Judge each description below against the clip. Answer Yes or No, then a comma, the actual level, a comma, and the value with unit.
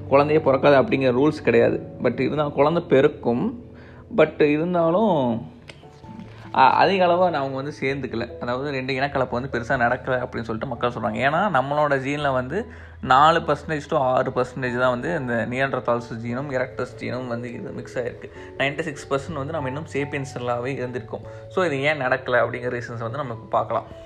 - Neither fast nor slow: No, fast, 155 wpm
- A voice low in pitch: Yes, low, 130 Hz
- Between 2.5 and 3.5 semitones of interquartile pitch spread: Yes, average, 2.9 semitones